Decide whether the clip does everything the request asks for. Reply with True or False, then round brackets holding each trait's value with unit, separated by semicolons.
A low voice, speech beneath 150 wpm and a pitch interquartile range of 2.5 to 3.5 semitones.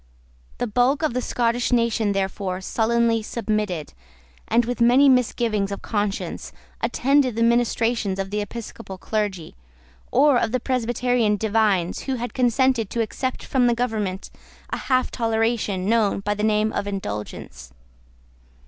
False (225 Hz; 140 wpm; 2.9 semitones)